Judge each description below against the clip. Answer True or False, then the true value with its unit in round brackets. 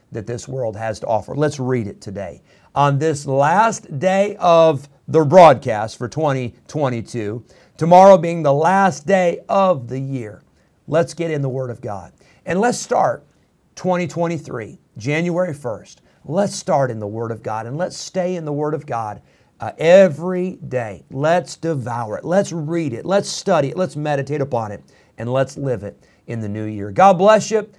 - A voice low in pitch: False (145 Hz)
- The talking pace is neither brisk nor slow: True (175 wpm)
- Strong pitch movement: True (6.3 semitones)